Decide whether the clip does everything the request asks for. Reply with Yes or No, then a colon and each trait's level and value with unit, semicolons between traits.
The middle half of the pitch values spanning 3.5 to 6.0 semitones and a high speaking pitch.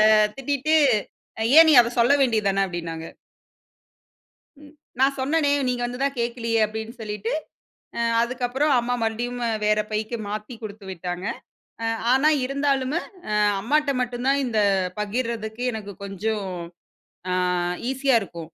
Yes: average, 4.0 semitones; high, 235 Hz